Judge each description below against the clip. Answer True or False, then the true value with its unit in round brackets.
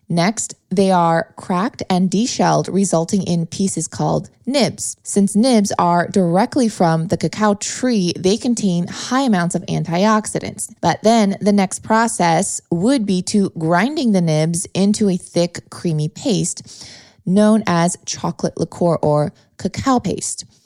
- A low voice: False (185 Hz)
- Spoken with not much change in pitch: False (4.0 semitones)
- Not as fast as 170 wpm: True (140 wpm)